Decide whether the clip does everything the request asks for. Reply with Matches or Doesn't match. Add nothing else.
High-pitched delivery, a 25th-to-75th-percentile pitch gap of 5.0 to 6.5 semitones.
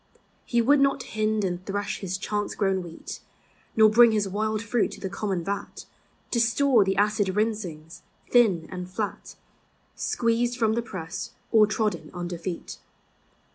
Doesn't match